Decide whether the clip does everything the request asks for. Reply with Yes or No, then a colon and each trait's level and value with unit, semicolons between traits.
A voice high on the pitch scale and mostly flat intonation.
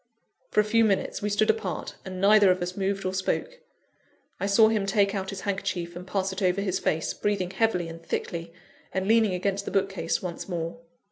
Yes: high, 195 Hz; narrow, 2.1 semitones